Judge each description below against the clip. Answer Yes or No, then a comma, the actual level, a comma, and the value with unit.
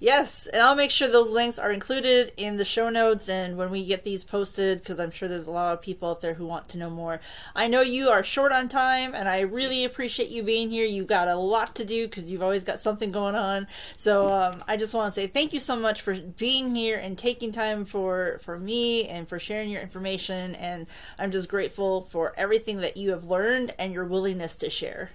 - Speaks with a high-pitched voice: Yes, high, 200 Hz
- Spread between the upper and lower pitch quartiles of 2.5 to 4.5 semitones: Yes, average, 3.7 semitones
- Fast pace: Yes, fast, 240 wpm